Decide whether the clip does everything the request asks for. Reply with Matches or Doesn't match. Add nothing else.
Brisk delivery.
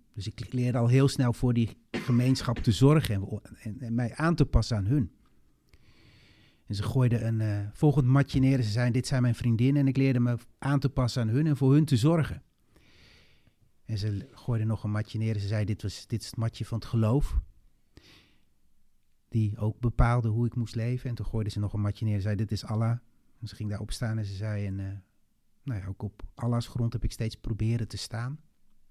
Matches